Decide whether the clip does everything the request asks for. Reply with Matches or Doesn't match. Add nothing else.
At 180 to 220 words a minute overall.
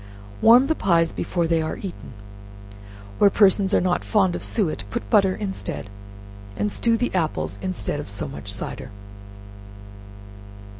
Doesn't match